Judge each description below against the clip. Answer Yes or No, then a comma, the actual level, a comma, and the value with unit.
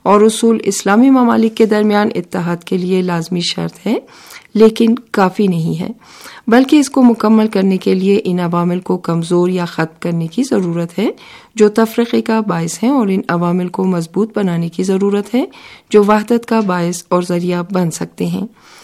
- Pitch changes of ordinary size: Yes, average, 4.2 semitones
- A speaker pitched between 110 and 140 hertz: No, high, 195 Hz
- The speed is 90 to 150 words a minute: No, average, 180 wpm